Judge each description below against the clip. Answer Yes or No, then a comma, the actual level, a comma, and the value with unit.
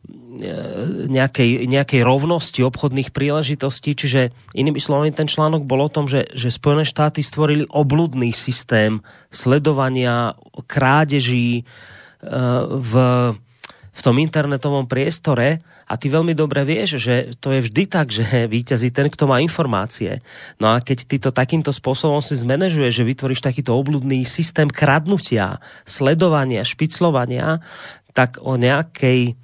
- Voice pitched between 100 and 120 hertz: No, low, 135 Hz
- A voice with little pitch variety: No, average, 3.4 semitones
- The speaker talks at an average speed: Yes, average, 125 wpm